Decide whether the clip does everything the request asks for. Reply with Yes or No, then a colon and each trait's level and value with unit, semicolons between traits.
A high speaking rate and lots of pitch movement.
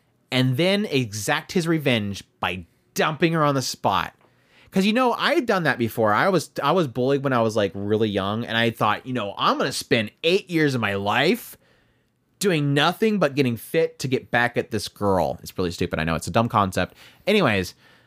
Yes: fast, 215 wpm; wide, 7.0 semitones